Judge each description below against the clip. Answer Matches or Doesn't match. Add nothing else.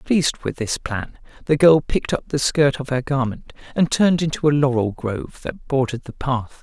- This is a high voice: Doesn't match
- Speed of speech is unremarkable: Doesn't match